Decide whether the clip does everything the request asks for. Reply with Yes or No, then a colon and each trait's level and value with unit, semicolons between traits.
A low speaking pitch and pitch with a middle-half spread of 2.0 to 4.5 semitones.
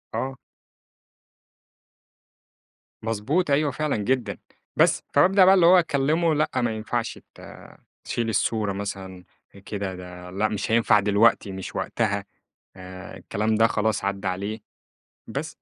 No: low, 110 Hz; average, 5.1 semitones